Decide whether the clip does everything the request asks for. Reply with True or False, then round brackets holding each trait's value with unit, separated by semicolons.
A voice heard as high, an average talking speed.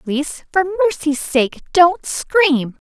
False (325 Hz; 125 wpm)